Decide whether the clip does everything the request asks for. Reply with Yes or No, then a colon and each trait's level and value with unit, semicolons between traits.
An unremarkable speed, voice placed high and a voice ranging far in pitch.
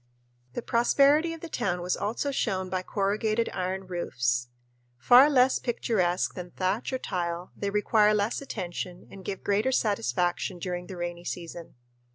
No: average, 155 wpm; high, 195 Hz; average, 4.5 semitones